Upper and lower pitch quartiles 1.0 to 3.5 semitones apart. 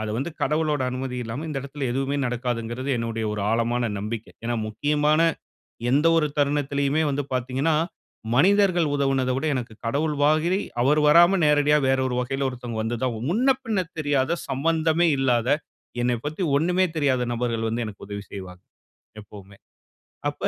No: average, 4.2 semitones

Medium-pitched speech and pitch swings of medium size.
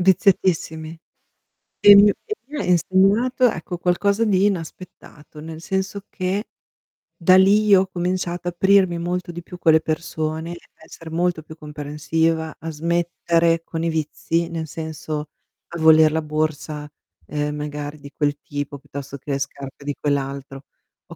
Yes: medium, 165 Hz; average, 3.2 semitones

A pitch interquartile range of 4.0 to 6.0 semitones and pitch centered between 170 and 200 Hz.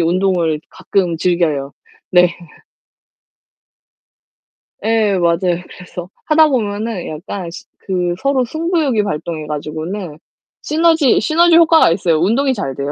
No: wide, 7.3 semitones; medium, 185 Hz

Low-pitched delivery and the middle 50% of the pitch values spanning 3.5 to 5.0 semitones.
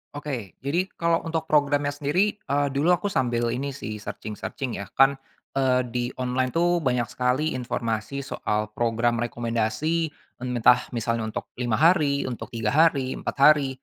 Yes: low, 130 Hz; average, 3.8 semitones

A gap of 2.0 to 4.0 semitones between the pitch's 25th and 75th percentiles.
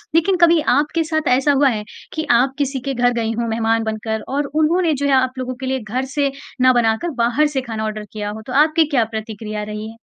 No: average, 4.6 semitones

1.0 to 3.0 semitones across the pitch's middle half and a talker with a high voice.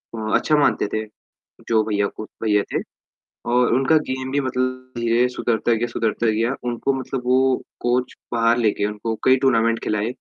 No: narrow, 2.4 semitones; low, 120 Hz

